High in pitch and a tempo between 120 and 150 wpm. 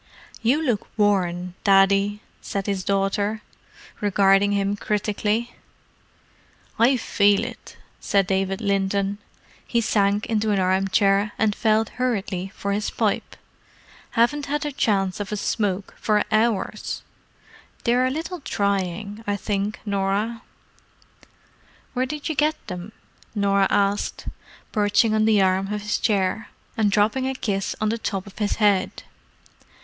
Yes: high, 205 Hz; slow, 135 wpm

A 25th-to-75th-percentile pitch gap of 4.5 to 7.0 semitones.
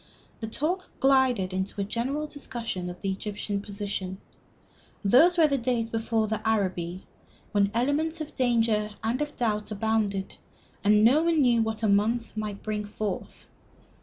No: average, 4.0 semitones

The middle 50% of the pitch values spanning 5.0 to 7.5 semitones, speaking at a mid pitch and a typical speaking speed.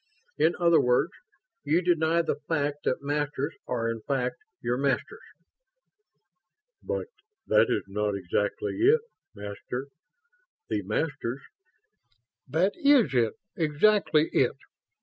No: average, 5.3 semitones; medium, 145 Hz; slow, 115 wpm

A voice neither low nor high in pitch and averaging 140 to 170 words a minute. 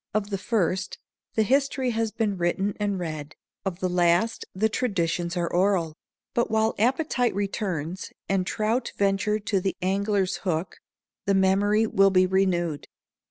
No: high, 195 Hz; average, 150 wpm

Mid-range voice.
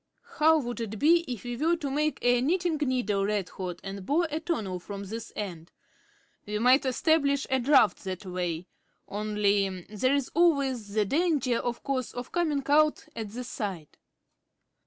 No: high, 245 Hz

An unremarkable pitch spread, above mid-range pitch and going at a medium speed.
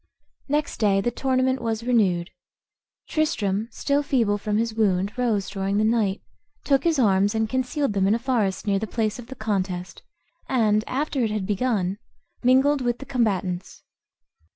Yes: average, 4.3 semitones; high, 220 Hz; average, 165 wpm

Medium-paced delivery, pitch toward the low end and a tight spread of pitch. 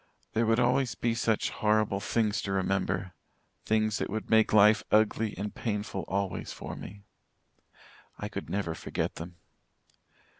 Yes: average, 145 wpm; low, 105 Hz; narrow, 2.1 semitones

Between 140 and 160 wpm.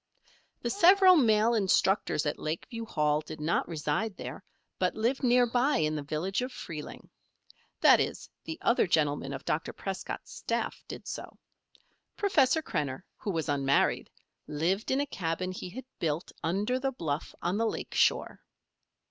Yes: average, 155 wpm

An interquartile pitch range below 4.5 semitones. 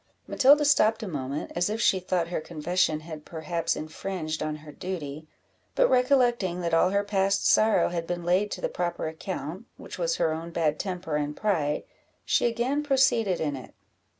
No: average, 5.2 semitones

